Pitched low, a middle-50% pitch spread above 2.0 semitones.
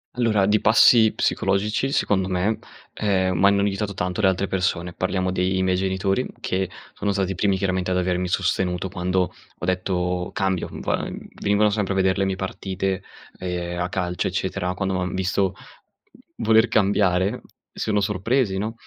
No: very low, 95 Hz; narrow, 1.7 semitones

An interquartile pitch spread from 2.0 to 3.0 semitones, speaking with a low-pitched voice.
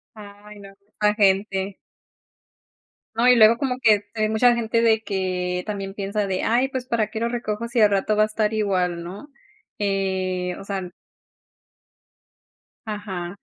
No: narrow, 2.4 semitones; high, 210 Hz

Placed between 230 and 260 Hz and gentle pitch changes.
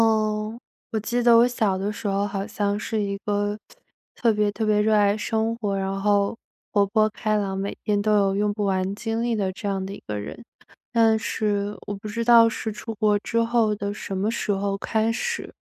No: high, 210 Hz; narrow, 1.8 semitones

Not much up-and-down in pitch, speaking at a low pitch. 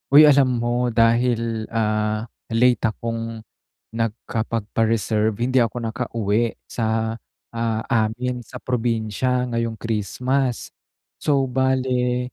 Yes: narrow, 1.9 semitones; low, 115 Hz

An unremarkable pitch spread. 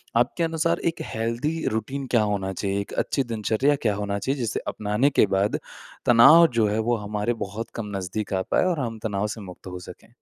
Yes: average, 4.2 semitones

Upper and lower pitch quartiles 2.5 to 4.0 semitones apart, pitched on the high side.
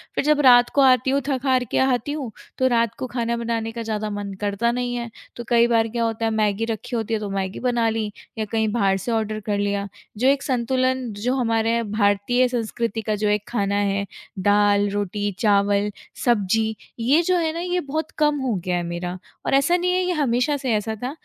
Yes: average, 3.7 semitones; high, 230 Hz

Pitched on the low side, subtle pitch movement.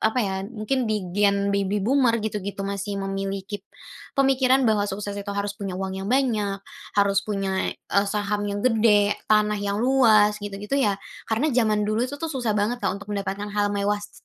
No: high, 205 Hz; narrow, 1.8 semitones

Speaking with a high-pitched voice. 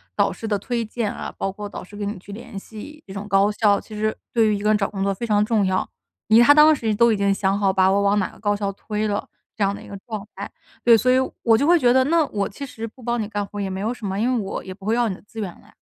Yes: high, 210 Hz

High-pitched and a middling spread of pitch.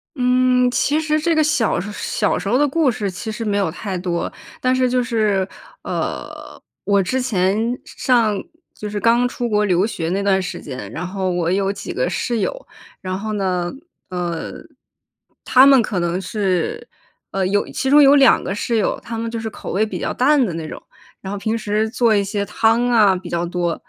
Yes: high, 210 Hz; average, 4.7 semitones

